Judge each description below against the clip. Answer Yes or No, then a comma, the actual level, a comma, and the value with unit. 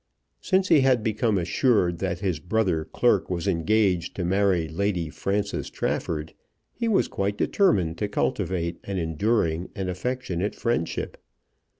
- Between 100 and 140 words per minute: Yes, slow, 135 wpm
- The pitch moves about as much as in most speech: Yes, average, 4.3 semitones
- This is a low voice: Yes, very low, 95 Hz